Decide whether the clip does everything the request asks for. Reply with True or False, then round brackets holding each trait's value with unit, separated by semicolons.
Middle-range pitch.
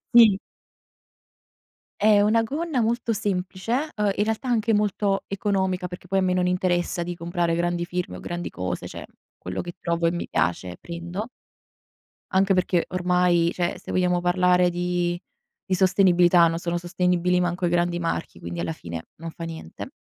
True (180 Hz)